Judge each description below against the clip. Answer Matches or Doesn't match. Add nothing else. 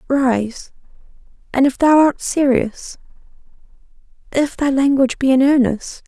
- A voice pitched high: Matches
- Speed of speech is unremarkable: Doesn't match